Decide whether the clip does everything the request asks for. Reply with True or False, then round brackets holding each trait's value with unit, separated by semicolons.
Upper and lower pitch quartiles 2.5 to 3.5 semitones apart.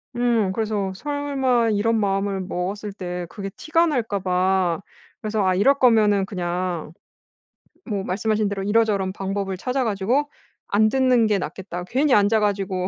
True (3.1 semitones)